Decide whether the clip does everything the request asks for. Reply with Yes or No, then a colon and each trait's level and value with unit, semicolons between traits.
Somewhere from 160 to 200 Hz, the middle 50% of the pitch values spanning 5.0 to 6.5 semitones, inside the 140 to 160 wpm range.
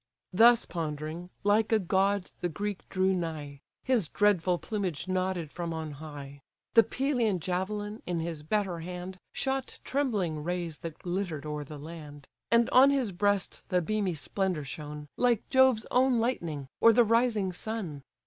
Yes: medium, 185 Hz; average, 5.3 semitones; average, 155 wpm